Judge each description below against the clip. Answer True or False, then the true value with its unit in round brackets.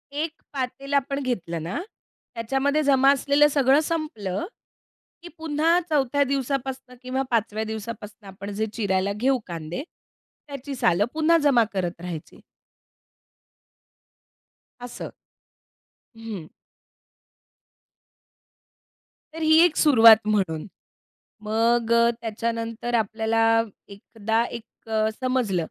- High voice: True (235 Hz)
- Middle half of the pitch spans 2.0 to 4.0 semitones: False (4.7 semitones)